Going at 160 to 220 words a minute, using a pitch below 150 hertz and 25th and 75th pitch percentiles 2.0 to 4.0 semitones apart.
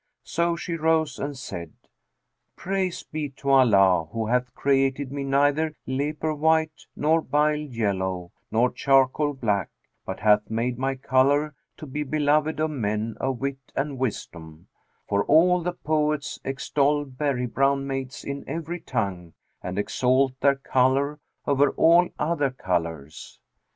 No: average, 140 wpm; low, 135 Hz; average, 3.7 semitones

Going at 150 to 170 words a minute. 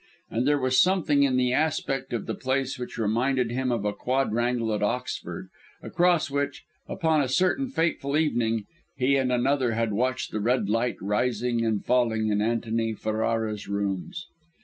Yes: average, 165 wpm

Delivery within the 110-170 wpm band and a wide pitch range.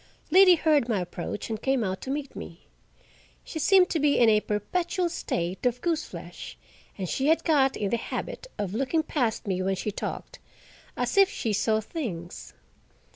No: average, 180 wpm; wide, 7.6 semitones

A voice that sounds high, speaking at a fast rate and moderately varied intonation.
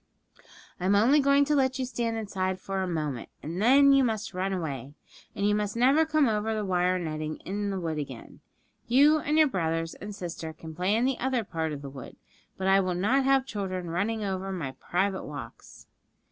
No: high, 195 Hz; fast, 210 wpm; wide, 6.3 semitones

